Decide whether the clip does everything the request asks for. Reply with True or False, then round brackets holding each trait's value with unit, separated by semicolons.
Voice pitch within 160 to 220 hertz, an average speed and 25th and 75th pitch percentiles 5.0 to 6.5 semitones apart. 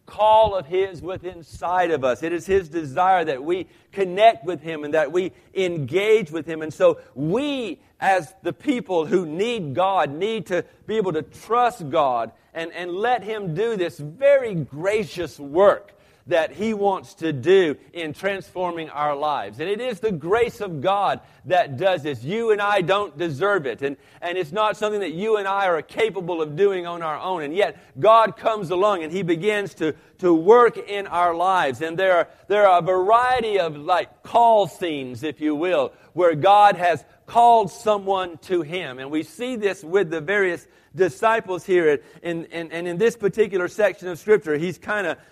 False (185 Hz; 190 wpm; 4.4 semitones)